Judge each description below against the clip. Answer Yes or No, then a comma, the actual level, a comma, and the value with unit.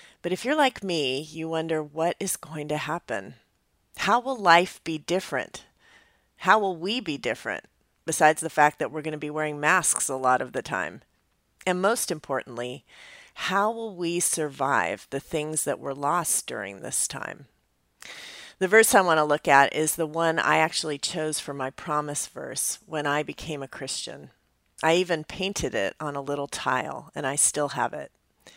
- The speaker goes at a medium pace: Yes, average, 185 wpm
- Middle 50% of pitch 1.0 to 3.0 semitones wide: No, average, 3.4 semitones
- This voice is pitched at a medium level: Yes, medium, 155 Hz